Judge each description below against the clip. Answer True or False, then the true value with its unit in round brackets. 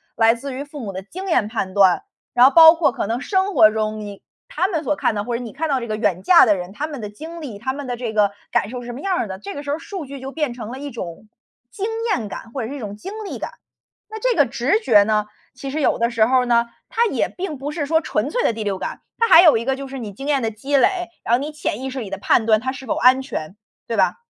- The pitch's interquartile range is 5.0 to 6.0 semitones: True (5.5 semitones)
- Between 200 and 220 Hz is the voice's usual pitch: False (255 Hz)